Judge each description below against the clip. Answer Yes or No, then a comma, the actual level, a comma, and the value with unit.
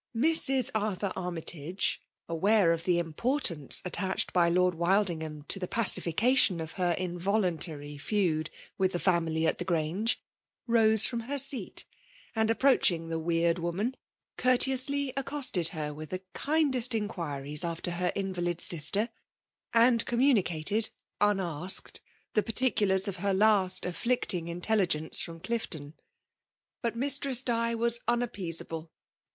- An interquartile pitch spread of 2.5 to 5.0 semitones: No, wide, 5.6 semitones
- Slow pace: Yes, slow, 130 wpm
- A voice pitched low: No, high, 190 Hz